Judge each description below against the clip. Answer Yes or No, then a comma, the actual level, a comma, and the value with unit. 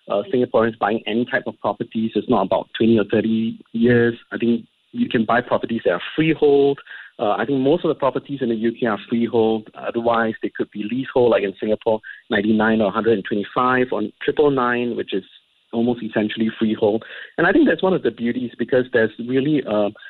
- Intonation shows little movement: Yes, narrow, 1.9 semitones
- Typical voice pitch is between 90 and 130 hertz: Yes, low, 115 Hz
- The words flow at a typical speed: No, fast, 220 wpm